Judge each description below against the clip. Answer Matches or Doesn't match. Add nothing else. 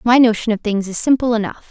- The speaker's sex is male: Doesn't match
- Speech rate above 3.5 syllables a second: Matches